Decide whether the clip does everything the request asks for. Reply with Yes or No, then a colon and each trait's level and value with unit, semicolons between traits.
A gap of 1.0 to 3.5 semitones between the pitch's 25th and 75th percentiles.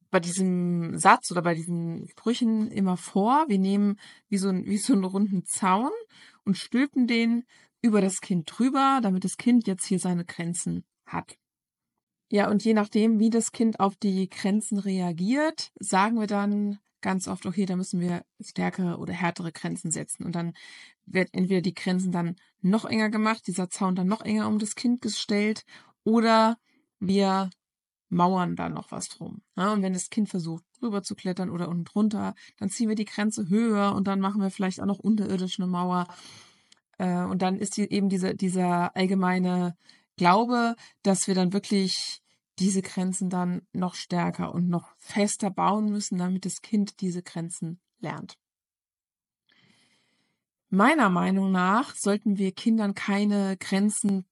Yes: narrow, 2.6 semitones